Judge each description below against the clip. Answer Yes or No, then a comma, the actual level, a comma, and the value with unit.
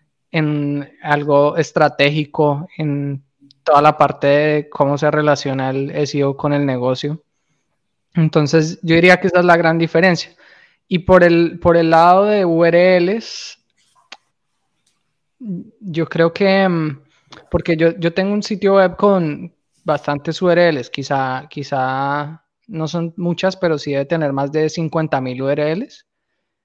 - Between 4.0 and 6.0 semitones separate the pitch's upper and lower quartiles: No, average, 3.2 semitones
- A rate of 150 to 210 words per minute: No, average, 135 wpm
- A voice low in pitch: No, medium, 160 Hz